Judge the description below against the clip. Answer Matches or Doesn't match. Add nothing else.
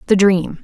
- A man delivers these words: Doesn't match